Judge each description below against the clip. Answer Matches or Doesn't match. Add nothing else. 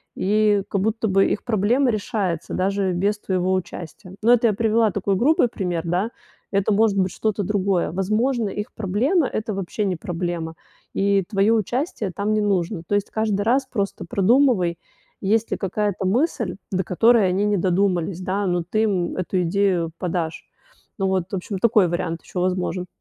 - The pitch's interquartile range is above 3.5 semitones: Doesn't match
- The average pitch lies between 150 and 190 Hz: Doesn't match